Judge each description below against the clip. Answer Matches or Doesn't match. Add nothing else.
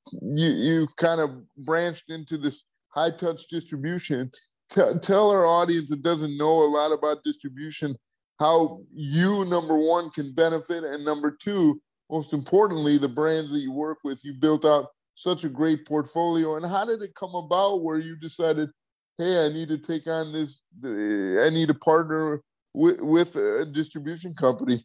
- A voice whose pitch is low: Doesn't match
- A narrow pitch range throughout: Matches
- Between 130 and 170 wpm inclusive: Matches